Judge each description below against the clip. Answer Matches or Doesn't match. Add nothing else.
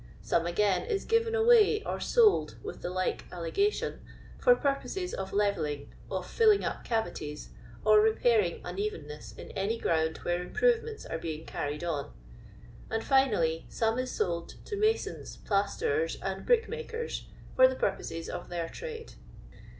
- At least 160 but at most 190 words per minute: Doesn't match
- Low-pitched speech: Doesn't match